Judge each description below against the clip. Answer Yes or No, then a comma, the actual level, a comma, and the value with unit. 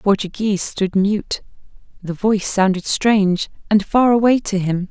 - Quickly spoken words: No, average, 145 wpm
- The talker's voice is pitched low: No, high, 200 Hz